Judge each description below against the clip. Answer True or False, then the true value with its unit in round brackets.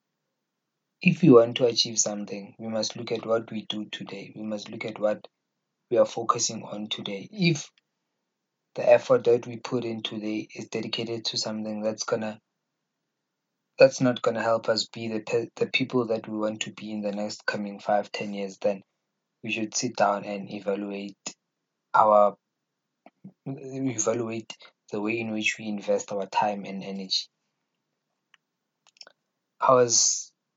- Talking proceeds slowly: False (155 wpm)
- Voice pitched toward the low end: True (110 Hz)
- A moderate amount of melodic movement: False (2.2 semitones)